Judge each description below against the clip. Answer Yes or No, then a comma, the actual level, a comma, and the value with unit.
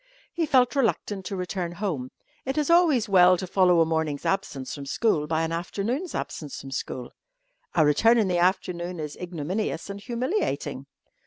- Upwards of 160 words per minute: Yes, average, 170 wpm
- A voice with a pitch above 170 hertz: Yes, medium, 185 Hz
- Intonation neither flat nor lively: No, wide, 5.7 semitones